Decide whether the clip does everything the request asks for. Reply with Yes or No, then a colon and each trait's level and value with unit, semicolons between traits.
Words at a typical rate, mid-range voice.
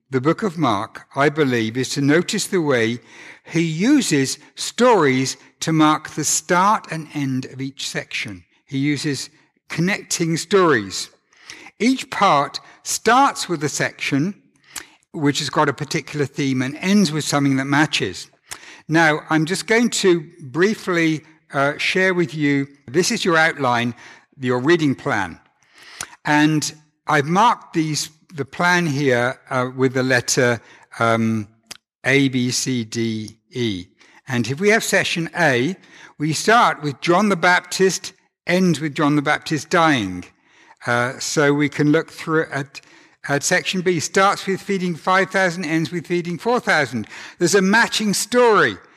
Yes: average, 150 wpm; medium, 155 Hz